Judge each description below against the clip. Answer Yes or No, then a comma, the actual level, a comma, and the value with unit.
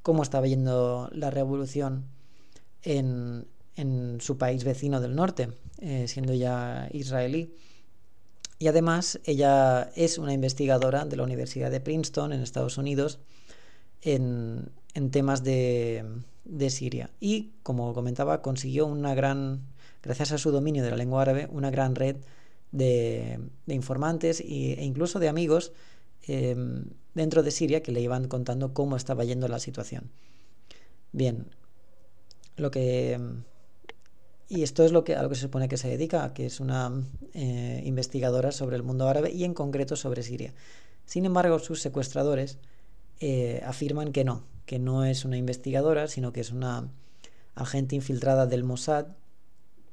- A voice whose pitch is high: No, low, 135 Hz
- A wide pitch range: No, average, 2.7 semitones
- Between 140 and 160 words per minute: Yes, average, 150 wpm